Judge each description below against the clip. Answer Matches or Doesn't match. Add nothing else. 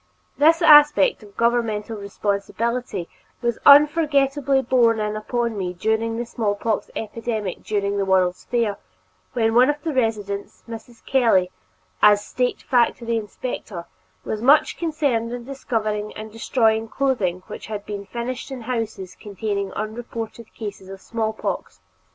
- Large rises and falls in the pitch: Doesn't match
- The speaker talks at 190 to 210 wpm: Doesn't match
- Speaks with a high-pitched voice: Matches